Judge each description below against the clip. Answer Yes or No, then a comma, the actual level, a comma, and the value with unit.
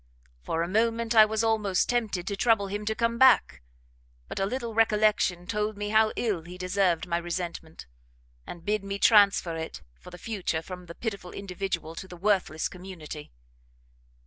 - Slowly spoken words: No, average, 170 wpm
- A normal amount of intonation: Yes, average, 3.7 semitones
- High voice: Yes, high, 195 Hz